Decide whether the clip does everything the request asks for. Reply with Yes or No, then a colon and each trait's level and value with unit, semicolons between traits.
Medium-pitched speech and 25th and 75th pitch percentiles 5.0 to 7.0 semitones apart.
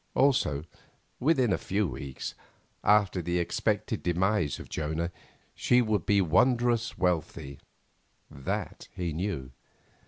No: very low, 90 Hz; average, 5.3 semitones